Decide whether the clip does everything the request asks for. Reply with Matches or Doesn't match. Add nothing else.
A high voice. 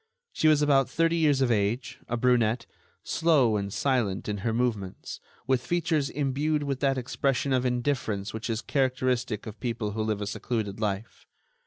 Doesn't match